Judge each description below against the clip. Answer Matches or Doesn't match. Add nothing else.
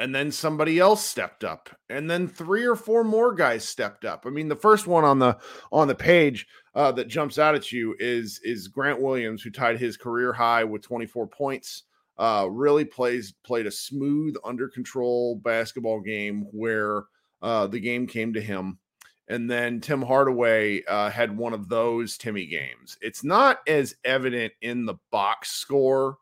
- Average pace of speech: Matches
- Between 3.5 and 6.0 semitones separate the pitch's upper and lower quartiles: Matches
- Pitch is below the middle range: Matches